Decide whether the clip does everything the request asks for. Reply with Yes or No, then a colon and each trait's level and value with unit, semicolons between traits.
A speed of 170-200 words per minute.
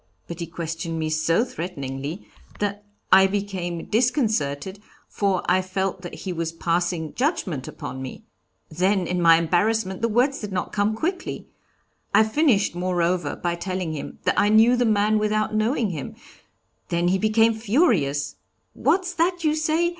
No: average, 155 wpm